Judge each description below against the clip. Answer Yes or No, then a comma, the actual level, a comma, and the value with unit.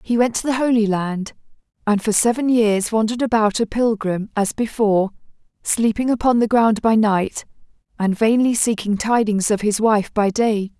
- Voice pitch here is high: Yes, high, 220 Hz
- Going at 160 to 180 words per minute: Yes, average, 170 wpm